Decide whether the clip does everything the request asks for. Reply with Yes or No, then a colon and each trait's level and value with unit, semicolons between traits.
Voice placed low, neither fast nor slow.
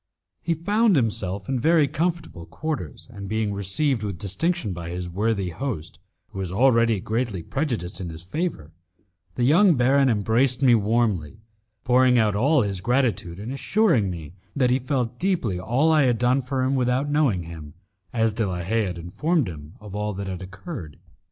Yes: low, 115 Hz; average, 175 wpm